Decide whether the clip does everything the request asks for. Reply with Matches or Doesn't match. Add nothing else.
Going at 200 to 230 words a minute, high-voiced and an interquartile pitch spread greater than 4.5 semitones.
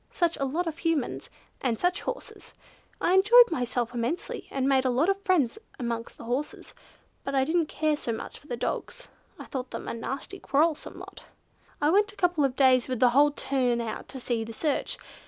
Matches